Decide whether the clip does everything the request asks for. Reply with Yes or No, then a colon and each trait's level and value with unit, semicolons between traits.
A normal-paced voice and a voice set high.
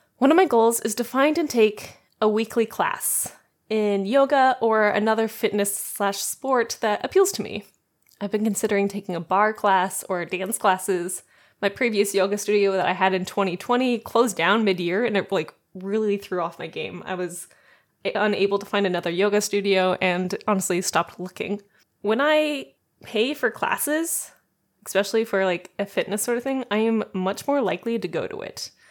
Yes: average, 180 wpm; high, 205 Hz